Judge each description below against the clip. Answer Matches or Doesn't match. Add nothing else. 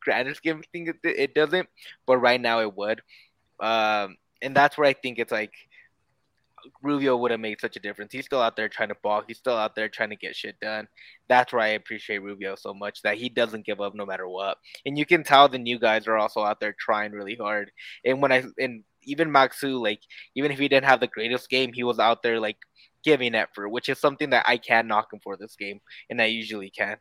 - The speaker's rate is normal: Doesn't match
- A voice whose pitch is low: Matches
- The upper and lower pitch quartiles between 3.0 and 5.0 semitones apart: Matches